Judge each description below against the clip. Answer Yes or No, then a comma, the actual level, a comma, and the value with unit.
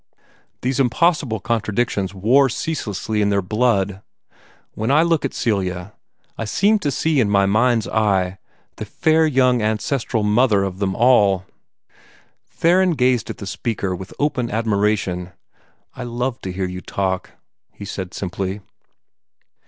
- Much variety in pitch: No, average, 4.6 semitones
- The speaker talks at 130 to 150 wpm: Yes, average, 140 wpm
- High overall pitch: No, low, 110 Hz